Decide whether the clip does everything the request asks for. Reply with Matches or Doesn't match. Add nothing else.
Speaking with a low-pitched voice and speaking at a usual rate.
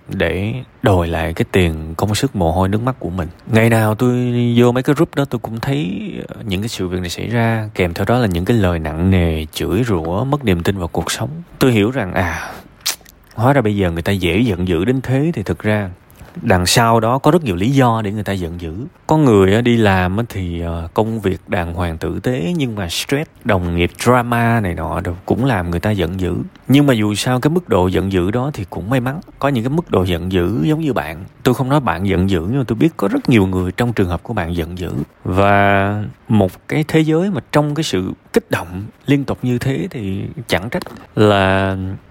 Matches